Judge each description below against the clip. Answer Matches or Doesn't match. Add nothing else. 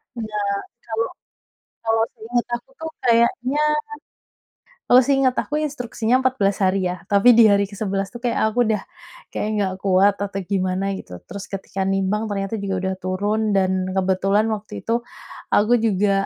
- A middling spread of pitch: Matches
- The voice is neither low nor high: Doesn't match